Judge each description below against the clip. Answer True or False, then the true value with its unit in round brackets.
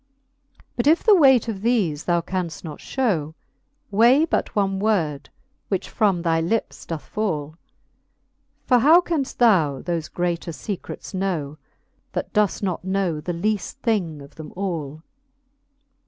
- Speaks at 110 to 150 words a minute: True (140 wpm)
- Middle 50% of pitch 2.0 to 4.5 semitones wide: False (5.3 semitones)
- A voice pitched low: False (185 Hz)